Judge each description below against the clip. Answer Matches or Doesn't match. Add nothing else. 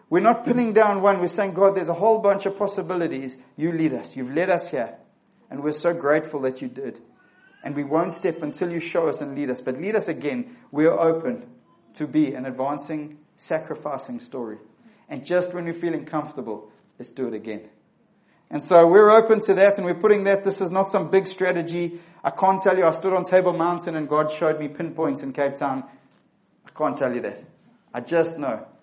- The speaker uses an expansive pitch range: Doesn't match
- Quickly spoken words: Matches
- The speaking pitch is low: Doesn't match